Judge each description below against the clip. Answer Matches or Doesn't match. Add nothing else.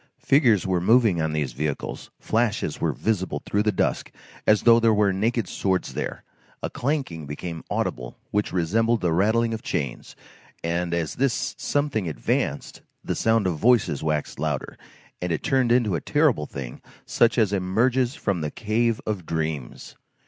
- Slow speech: Doesn't match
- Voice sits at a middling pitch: Doesn't match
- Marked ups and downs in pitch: Matches